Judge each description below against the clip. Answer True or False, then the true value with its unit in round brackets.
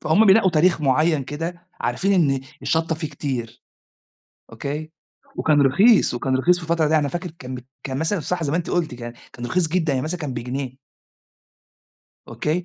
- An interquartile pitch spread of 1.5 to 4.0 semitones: False (4.4 semitones)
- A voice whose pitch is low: False (155 Hz)